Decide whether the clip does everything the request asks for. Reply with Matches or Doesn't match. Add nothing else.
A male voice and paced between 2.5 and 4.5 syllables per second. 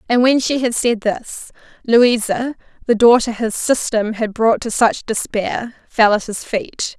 Doesn't match